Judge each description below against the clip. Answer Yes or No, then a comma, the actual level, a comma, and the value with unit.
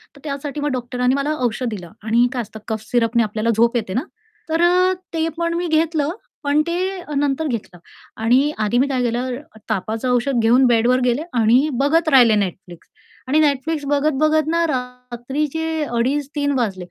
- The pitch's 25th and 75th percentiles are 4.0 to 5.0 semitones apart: Yes, average, 4.6 semitones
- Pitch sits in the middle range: No, very high, 260 Hz